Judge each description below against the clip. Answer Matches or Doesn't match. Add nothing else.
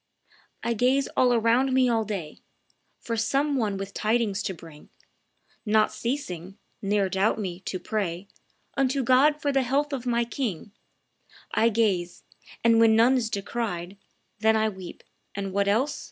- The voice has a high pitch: Matches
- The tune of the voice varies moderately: Matches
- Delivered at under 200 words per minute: Matches